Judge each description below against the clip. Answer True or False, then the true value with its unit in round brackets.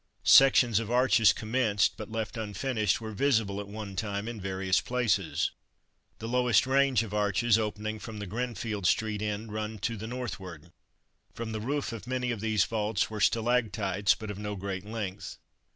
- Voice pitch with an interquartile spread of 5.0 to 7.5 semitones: False (2.4 semitones)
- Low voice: True (110 Hz)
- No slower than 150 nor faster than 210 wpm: True (170 wpm)